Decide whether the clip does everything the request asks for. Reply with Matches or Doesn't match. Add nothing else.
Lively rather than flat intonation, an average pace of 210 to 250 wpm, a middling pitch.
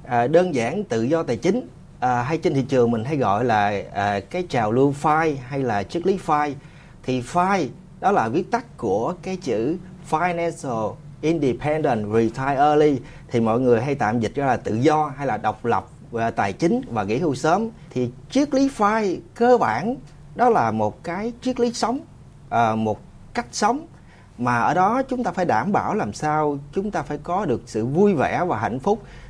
Doesn't match